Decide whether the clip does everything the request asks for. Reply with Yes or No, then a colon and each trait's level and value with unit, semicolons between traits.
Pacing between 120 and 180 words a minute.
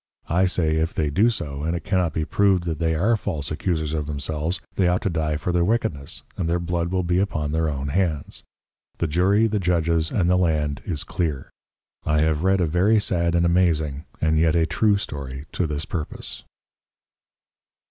No: average, 200 wpm